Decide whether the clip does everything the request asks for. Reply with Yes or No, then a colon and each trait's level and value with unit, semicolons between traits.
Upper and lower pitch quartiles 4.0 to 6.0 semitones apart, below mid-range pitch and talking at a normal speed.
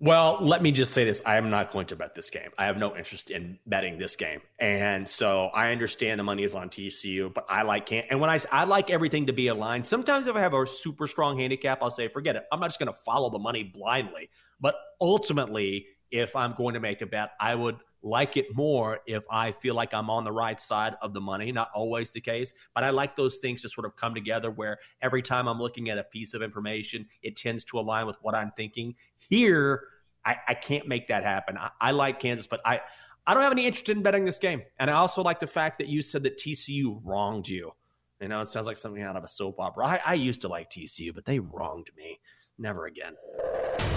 No: average, 4.8 semitones; low, 120 Hz; fast, 245 wpm